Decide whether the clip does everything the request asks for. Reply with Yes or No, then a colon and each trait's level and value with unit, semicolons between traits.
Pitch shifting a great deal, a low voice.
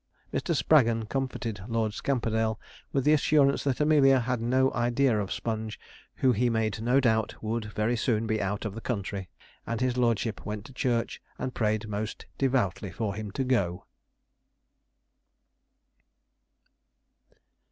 No: average, 3.1 semitones; low, 115 Hz